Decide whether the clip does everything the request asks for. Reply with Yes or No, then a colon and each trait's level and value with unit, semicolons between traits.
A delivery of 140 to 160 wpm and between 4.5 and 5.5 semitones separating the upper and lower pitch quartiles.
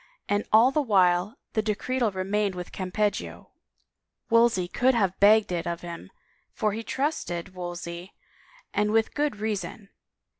No: average, 145 wpm; average, 3.7 semitones